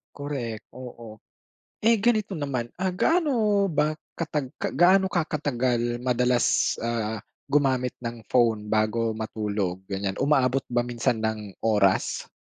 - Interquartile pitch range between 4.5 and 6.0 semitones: Yes, average, 5.2 semitones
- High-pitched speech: No, low, 125 Hz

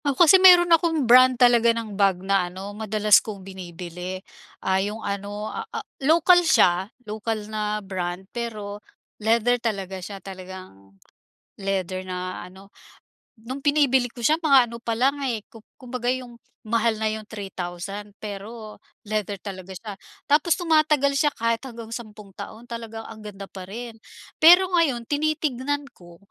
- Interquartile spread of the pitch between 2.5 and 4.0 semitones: No, average, 4.6 semitones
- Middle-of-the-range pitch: No, high, 220 Hz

